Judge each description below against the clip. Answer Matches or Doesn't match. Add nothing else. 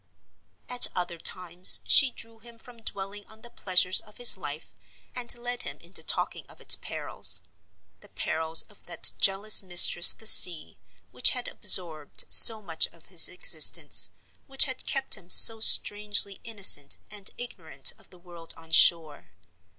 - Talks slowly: Doesn't match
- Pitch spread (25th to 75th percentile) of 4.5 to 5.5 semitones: Matches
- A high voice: Matches